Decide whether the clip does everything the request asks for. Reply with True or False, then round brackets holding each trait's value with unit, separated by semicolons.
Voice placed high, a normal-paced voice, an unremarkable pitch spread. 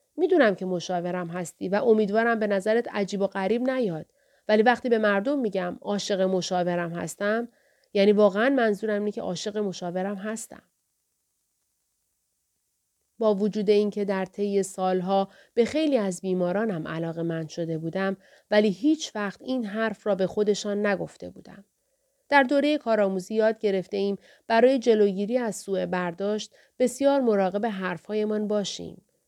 True (205 Hz; 135 wpm; 3.1 semitones)